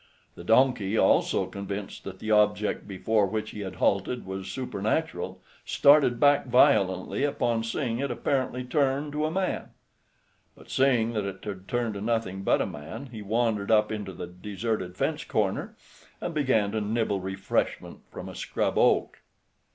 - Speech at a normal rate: Yes, average, 160 wpm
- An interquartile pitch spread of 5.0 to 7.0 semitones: No, average, 4.2 semitones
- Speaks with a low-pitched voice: Yes, low, 110 Hz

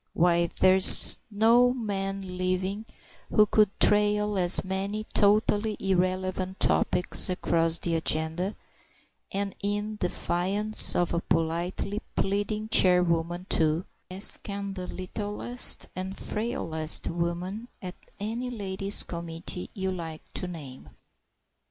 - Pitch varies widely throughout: No, average, 2.8 semitones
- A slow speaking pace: Yes, slow, 110 wpm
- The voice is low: No, high, 190 Hz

